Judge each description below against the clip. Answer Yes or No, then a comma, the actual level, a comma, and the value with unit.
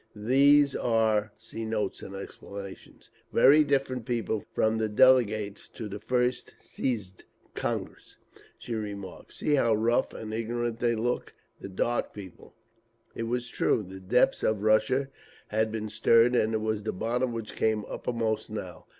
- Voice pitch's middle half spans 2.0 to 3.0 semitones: Yes, narrow, 2.4 semitones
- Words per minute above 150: No, average, 140 wpm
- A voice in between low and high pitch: No, low, 110 Hz